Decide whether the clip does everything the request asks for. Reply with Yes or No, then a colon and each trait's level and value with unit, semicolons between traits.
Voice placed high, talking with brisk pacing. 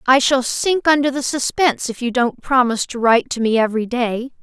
Yes: very high, 250 Hz; fast, 215 wpm